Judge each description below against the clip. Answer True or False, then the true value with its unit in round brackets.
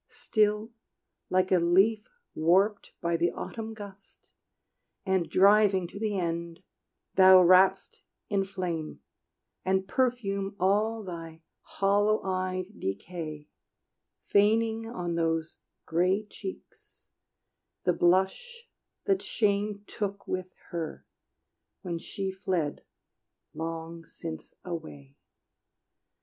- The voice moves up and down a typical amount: True (3.5 semitones)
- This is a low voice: False (190 Hz)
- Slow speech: True (100 wpm)